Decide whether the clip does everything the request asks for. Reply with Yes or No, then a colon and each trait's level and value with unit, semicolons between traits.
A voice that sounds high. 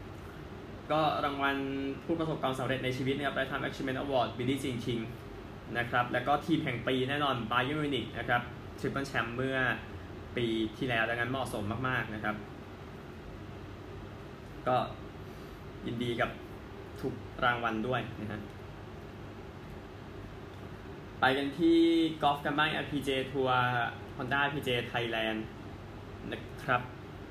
No: low, 120 Hz